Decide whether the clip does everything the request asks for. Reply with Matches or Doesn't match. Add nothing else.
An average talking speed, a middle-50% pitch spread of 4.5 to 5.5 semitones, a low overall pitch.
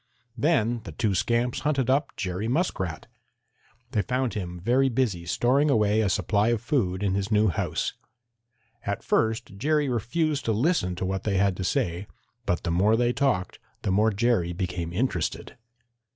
Matches